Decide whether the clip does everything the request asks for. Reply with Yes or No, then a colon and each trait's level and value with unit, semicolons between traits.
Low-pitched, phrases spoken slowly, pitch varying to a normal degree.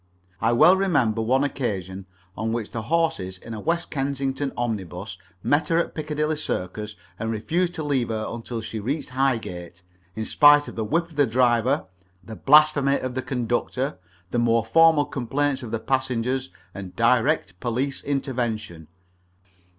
No: low, 125 Hz; average, 160 wpm; average, 4.5 semitones